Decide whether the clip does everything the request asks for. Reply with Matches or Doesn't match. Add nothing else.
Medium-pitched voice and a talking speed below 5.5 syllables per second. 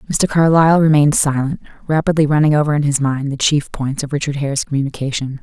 Doesn't match